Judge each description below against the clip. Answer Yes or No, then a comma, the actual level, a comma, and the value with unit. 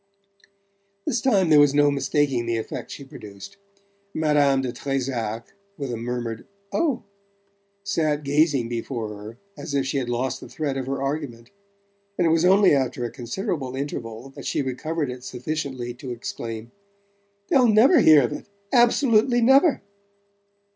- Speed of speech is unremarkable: Yes, average, 155 wpm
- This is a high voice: No, low, 135 Hz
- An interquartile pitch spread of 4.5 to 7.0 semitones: Yes, average, 5.0 semitones